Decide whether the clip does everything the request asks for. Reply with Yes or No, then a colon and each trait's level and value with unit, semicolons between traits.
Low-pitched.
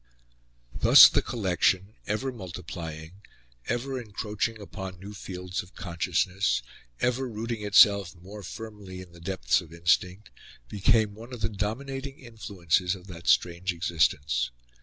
Yes: very low, 95 Hz